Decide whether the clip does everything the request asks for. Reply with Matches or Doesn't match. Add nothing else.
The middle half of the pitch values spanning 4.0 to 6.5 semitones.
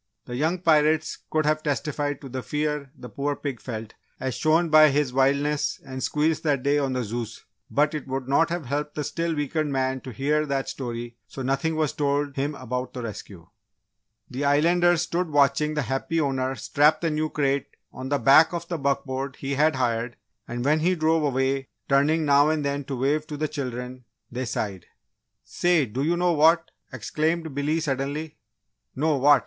Doesn't match